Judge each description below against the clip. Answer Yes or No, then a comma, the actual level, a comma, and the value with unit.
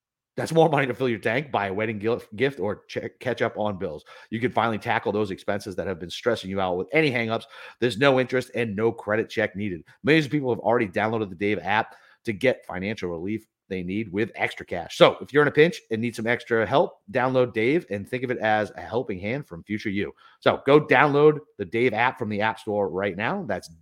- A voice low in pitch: Yes, low, 115 Hz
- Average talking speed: No, fast, 240 wpm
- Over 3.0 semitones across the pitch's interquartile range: Yes, average, 3.6 semitones